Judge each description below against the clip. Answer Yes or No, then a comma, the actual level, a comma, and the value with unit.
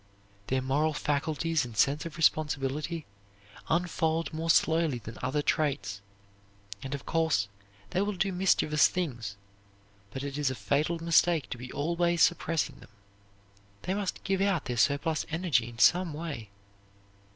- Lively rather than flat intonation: No, average, 3.9 semitones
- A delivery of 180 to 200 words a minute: No, average, 145 wpm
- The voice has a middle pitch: Yes, medium, 155 Hz